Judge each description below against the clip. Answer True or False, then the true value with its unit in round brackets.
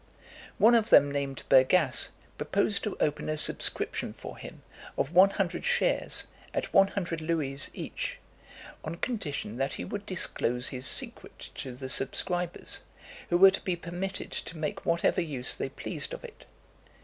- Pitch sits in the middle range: True (170 Hz)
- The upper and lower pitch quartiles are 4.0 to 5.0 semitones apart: False (5.6 semitones)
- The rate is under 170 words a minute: True (160 wpm)